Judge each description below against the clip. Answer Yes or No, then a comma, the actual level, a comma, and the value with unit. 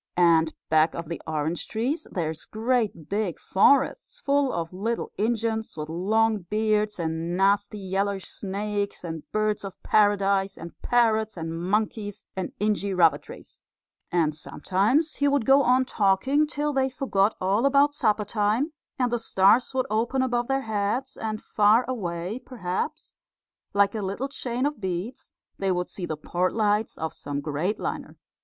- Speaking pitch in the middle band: No, high, 205 Hz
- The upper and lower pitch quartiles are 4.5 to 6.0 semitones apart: Yes, average, 4.8 semitones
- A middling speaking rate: Yes, average, 160 wpm